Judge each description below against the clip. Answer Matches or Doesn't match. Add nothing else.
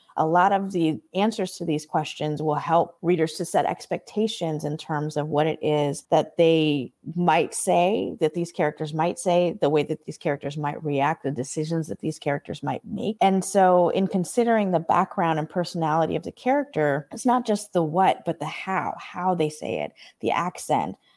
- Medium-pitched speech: Matches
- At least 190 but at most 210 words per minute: Matches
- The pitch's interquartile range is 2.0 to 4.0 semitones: Matches